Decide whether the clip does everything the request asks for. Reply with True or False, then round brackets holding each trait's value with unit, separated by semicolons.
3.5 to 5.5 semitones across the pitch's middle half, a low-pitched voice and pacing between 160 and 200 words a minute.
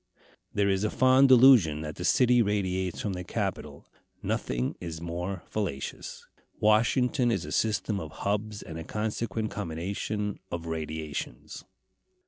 False (4.9 semitones; 100 Hz; 135 wpm)